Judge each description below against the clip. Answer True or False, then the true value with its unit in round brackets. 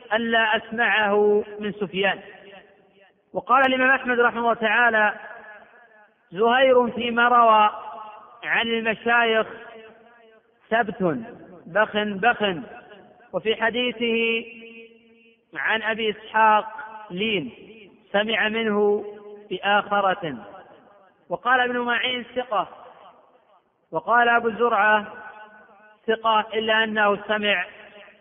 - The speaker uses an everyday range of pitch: False (2.0 semitones)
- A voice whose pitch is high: True (220 Hz)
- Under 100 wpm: True (80 wpm)